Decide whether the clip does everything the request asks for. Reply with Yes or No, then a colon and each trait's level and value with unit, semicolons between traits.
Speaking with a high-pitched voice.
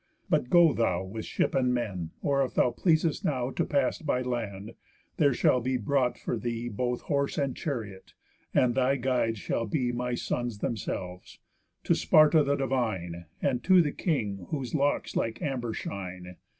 No: low, 125 Hz